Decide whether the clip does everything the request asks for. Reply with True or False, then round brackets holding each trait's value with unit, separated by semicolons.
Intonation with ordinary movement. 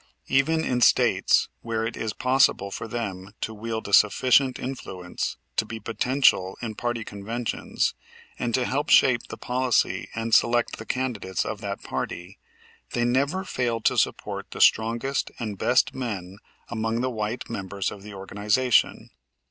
True (3.6 semitones)